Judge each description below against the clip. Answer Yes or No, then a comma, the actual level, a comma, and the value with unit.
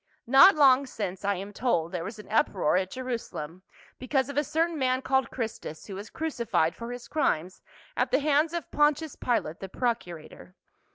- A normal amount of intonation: No, wide, 6.7 semitones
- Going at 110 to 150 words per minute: No, average, 180 wpm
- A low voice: No, high, 240 Hz